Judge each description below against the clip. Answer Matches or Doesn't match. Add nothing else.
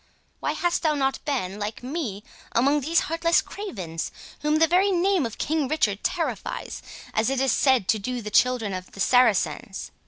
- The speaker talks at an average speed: Matches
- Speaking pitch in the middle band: Doesn't match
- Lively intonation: Matches